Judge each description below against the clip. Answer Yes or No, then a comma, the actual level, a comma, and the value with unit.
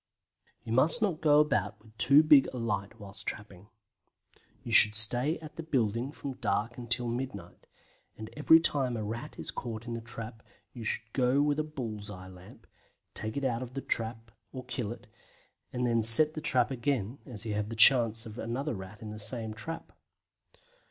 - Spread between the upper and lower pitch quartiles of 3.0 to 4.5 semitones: Yes, average, 3.8 semitones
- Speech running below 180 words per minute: No, average, 190 wpm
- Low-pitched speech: Yes, low, 115 Hz